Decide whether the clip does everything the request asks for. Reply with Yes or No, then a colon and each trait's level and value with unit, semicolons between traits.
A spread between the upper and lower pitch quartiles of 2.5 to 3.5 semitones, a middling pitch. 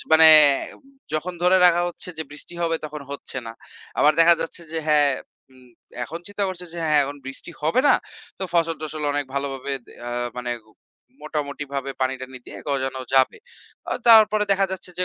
No: average, 3.9 semitones; medium, 155 Hz